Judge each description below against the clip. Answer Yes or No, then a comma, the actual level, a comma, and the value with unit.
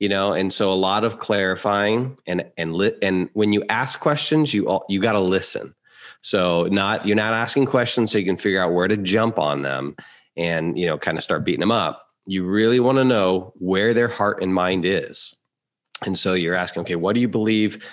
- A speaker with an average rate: No, fast, 220 wpm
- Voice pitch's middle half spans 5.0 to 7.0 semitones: No, average, 3.4 semitones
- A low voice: Yes, low, 100 Hz